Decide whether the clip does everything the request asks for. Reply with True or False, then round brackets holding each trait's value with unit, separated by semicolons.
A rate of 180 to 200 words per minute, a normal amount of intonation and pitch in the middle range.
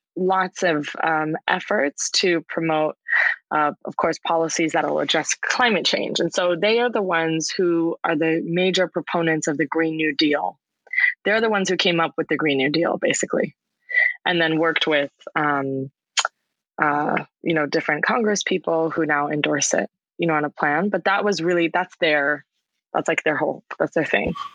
True (185 wpm; 3.0 semitones; 165 Hz)